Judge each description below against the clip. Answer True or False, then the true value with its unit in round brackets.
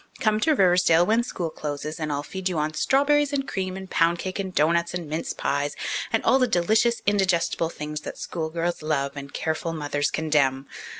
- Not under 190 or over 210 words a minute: True (195 wpm)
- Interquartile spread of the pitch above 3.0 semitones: True (4.2 semitones)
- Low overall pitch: False (170 Hz)